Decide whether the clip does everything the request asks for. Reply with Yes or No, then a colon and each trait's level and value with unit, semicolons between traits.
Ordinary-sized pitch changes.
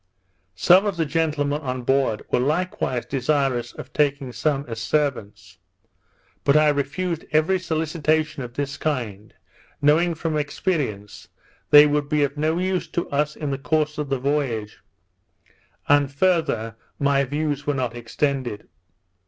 Yes: average, 3.1 semitones